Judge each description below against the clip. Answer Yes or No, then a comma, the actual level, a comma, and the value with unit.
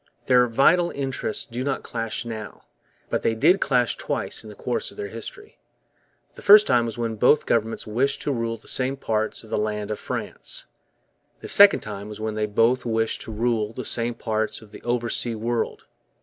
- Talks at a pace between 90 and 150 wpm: No, average, 195 wpm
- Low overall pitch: Yes, low, 115 Hz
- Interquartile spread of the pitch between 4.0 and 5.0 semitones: No, average, 2.7 semitones